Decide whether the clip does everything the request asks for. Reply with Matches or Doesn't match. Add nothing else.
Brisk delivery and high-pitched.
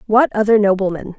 Doesn't match